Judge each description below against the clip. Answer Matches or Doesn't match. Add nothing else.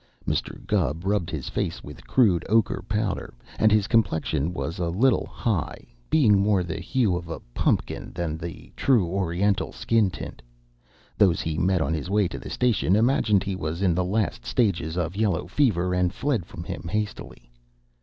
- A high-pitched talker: Doesn't match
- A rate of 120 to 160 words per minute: Doesn't match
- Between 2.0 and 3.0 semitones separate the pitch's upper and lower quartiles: Doesn't match